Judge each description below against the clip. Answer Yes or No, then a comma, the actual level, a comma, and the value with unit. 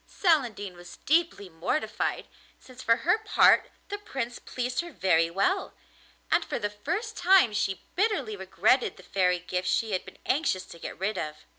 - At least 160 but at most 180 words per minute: Yes, average, 170 wpm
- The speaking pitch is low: No, high, 230 Hz